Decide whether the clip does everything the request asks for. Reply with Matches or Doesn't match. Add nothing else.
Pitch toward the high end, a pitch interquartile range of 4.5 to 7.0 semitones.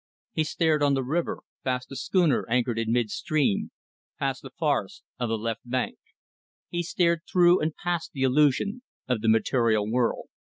Doesn't match